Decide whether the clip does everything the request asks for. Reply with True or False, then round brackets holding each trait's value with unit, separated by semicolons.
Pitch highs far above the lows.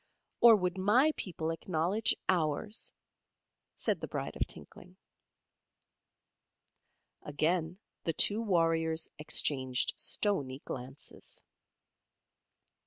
False (4.0 semitones)